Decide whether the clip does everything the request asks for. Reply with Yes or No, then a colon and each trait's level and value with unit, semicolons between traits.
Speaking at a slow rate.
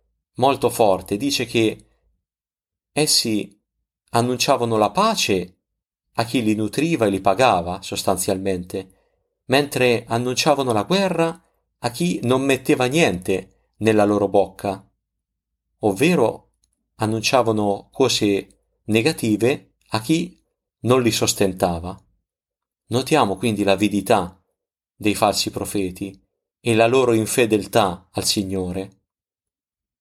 Yes: slow, 100 wpm